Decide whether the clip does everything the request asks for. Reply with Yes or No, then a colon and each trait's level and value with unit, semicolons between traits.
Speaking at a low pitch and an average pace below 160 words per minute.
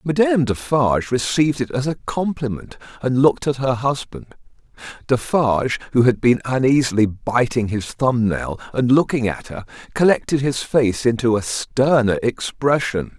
Yes: low, 125 Hz; average, 145 wpm